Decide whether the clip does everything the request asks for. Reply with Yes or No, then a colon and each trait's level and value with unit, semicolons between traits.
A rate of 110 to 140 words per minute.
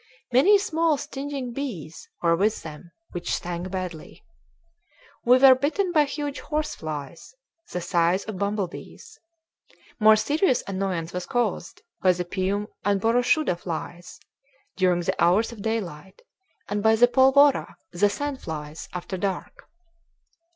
Yes: slow, 135 wpm